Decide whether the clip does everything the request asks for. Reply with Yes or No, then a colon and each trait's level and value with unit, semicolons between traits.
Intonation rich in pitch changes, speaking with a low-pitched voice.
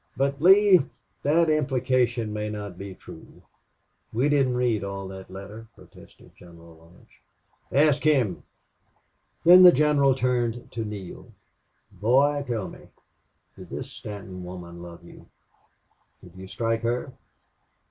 Yes: wide, 6.3 semitones; low, 115 Hz